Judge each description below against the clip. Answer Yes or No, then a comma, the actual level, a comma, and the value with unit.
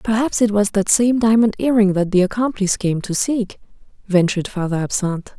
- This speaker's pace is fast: No, average, 180 wpm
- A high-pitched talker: Yes, high, 205 Hz